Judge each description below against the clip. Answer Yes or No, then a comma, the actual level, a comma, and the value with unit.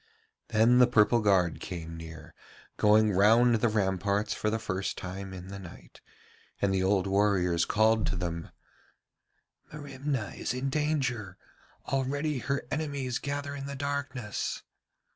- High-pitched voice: No, low, 110 Hz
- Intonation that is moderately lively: No, wide, 5.8 semitones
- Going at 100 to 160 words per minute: Yes, average, 140 wpm